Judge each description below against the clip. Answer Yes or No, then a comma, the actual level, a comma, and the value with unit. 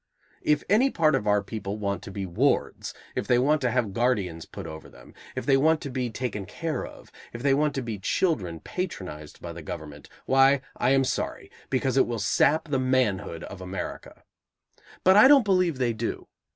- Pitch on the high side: No, low, 125 Hz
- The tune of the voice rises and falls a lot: Yes, wide, 6.6 semitones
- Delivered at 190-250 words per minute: Yes, average, 200 wpm